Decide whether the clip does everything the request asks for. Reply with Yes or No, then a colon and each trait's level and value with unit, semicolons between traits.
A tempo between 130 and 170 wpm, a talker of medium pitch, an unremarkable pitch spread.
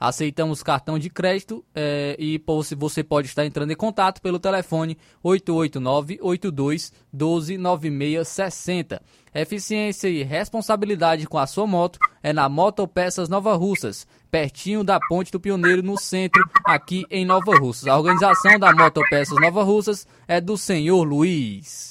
Yes: average, 135 wpm; medium, 175 Hz; average, 3.9 semitones